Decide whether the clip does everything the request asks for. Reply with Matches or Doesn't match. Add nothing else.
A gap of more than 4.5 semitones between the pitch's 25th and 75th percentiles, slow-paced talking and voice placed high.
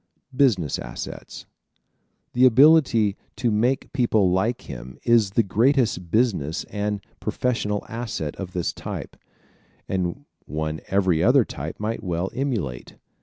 Doesn't match